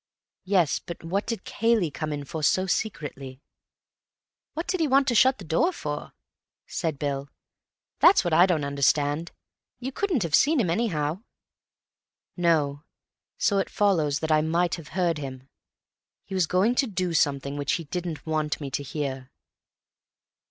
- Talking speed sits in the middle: Yes, average, 160 wpm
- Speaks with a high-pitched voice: No, medium, 165 Hz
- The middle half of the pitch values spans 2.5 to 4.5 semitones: No, average, 5.0 semitones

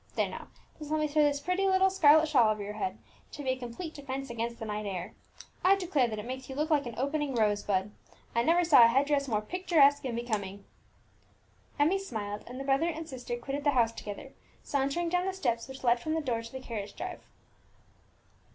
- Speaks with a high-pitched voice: Yes, very high, 270 Hz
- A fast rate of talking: Yes, fast, 220 wpm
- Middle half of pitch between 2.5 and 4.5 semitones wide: No, average, 5.0 semitones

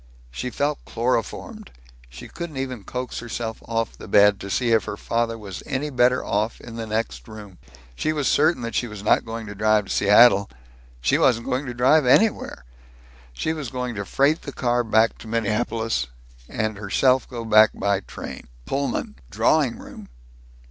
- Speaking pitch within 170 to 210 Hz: No, low, 115 Hz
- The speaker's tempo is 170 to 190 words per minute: Yes, average, 175 wpm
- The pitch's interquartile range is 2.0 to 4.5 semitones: Yes, average, 3.0 semitones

